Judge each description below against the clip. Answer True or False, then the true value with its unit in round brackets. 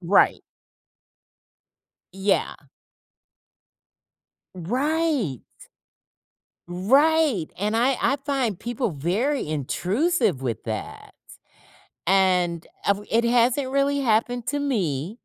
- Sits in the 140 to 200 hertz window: False (225 Hz)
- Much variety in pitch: True (7.4 semitones)